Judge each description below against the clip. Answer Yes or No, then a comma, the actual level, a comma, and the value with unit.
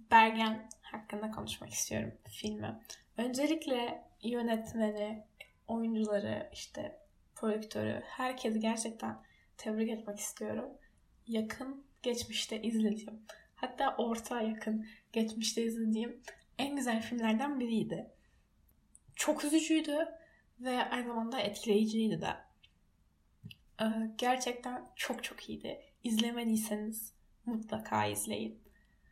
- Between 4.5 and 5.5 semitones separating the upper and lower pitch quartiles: No, narrow, 2.4 semitones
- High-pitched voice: Yes, high, 220 Hz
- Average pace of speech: No, slow, 85 wpm